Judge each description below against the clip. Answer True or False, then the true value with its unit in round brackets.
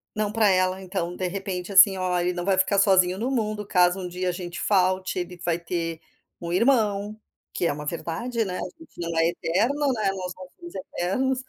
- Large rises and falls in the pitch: False (2.9 semitones)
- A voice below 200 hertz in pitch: True (185 Hz)